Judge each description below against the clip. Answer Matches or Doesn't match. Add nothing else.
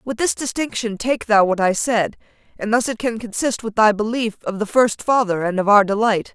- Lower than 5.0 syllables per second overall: Doesn't match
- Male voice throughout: Doesn't match